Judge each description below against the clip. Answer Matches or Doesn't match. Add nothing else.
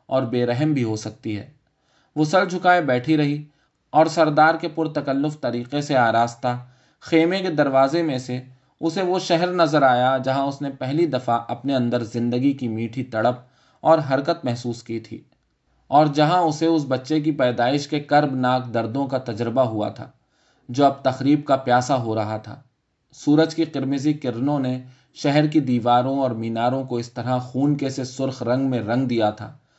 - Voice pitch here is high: Doesn't match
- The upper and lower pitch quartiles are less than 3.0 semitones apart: Doesn't match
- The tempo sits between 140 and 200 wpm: Matches